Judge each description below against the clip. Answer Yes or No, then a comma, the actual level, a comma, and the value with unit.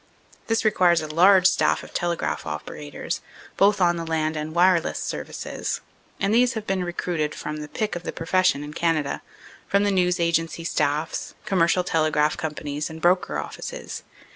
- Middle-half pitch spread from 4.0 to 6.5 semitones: No, average, 3.2 semitones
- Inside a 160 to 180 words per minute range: Yes, average, 165 wpm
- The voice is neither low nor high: Yes, medium, 170 Hz